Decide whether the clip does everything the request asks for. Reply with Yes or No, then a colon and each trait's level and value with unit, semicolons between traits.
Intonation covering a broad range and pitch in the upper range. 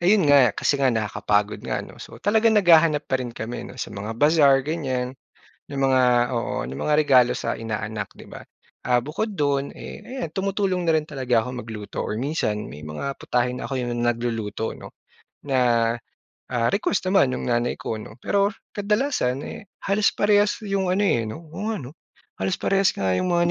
No: wide, 7.7 semitones; low, 135 Hz